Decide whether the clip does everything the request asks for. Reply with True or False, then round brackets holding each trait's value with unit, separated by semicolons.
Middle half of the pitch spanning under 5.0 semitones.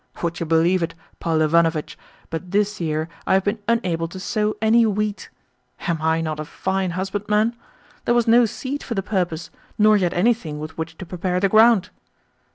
True (4.4 semitones)